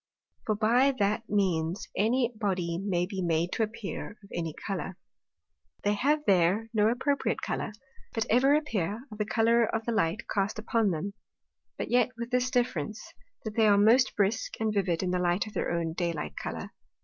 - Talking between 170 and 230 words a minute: Yes, average, 185 wpm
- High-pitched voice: Yes, high, 210 Hz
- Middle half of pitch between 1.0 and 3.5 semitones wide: No, average, 3.9 semitones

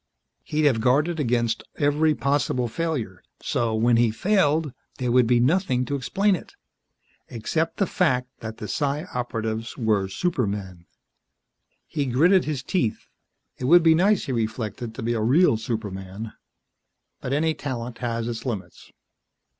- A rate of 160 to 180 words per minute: No, average, 145 wpm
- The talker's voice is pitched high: No, low, 125 Hz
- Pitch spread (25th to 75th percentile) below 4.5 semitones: No, average, 5.2 semitones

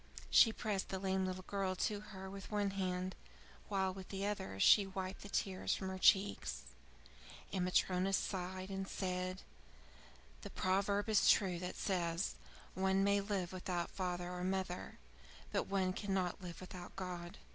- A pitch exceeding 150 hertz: Yes, high, 190 Hz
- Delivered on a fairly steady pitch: Yes, narrow, 1.3 semitones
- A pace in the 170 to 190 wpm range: No, average, 155 wpm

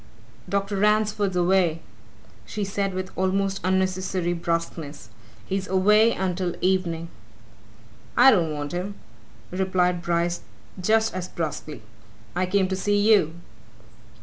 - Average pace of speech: No, slow, 120 wpm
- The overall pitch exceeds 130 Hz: Yes, medium, 185 Hz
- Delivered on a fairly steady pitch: Yes, narrow, 2.2 semitones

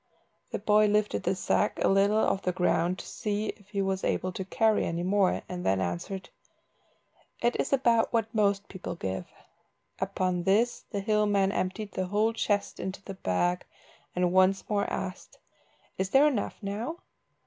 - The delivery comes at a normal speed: Yes, average, 170 wpm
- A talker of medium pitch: No, high, 195 Hz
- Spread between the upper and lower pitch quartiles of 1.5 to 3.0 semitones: Yes, narrow, 2.4 semitones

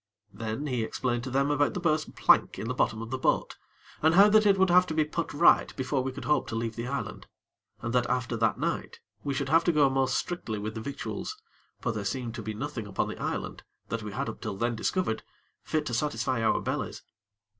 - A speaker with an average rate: No, fast, 235 wpm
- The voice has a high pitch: No, low, 130 Hz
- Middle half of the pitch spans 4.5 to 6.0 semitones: Yes, average, 4.9 semitones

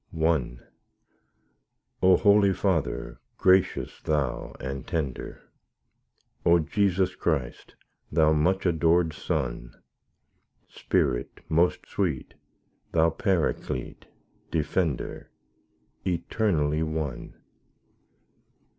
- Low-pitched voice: Yes, very low, 80 Hz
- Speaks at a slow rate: Yes, slow, 75 wpm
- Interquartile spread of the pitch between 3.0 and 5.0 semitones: Yes, average, 3.9 semitones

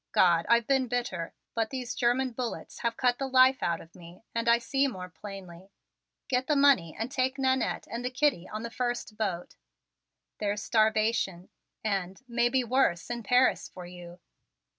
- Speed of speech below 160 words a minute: No, average, 170 wpm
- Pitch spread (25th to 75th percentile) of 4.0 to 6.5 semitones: Yes, average, 5.2 semitones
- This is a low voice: No, high, 235 Hz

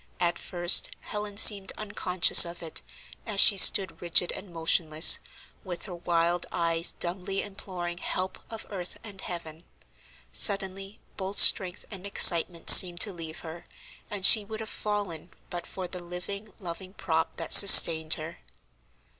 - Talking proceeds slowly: No, average, 145 wpm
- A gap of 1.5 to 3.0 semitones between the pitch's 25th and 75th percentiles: Yes, narrow, 2.6 semitones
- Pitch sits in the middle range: Yes, medium, 180 Hz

